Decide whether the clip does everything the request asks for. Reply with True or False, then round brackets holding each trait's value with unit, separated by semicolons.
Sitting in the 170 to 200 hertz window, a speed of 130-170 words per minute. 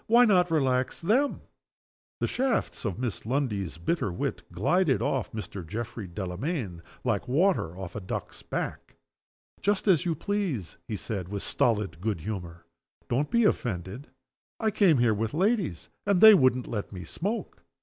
False (125 Hz; 155 wpm)